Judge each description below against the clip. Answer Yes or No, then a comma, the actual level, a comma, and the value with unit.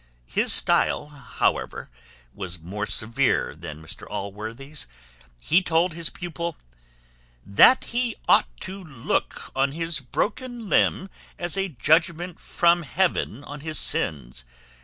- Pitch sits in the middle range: Yes, medium, 155 Hz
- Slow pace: Yes, slow, 120 wpm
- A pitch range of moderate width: No, wide, 8.1 semitones